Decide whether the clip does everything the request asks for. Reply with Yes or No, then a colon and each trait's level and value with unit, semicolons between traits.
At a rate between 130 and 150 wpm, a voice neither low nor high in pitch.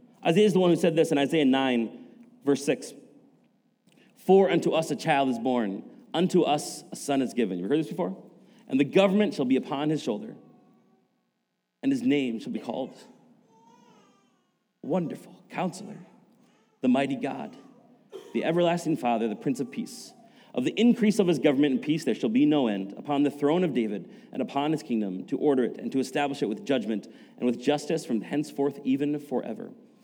No: average, 185 wpm; medium, 155 Hz